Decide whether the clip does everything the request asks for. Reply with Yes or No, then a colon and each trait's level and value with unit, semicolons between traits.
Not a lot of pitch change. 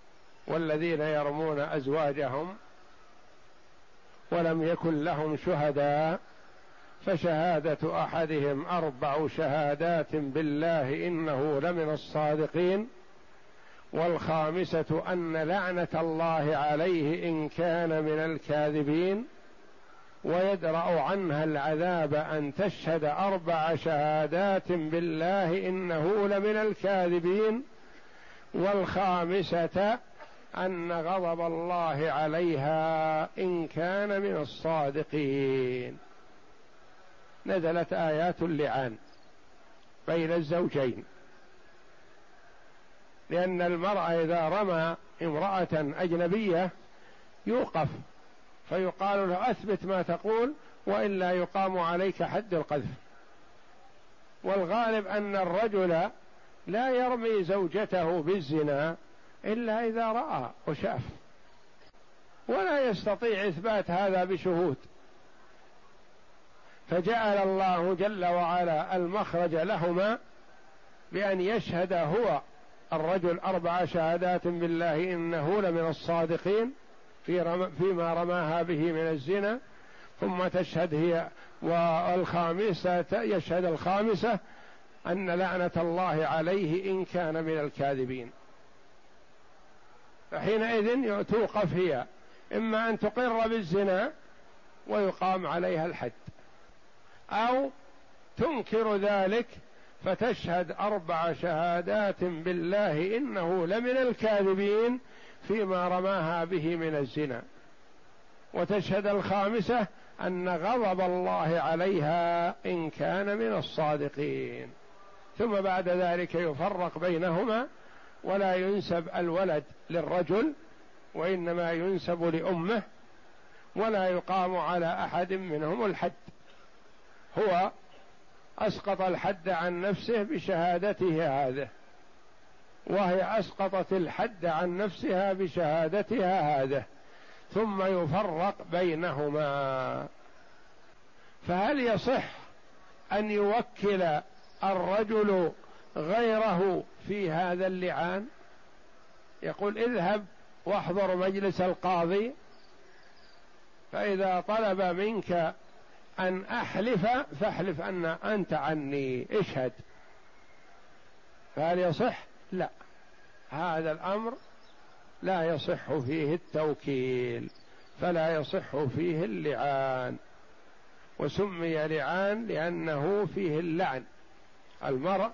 No: average, 3.3 semitones